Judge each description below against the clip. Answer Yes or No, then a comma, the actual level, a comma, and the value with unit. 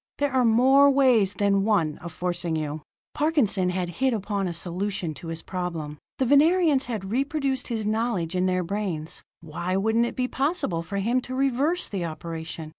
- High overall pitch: Yes, high, 200 Hz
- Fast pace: No, average, 180 wpm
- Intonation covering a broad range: Yes, wide, 6.9 semitones